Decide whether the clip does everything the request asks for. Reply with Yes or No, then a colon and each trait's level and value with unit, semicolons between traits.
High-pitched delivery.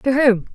Yes: high, 245 Hz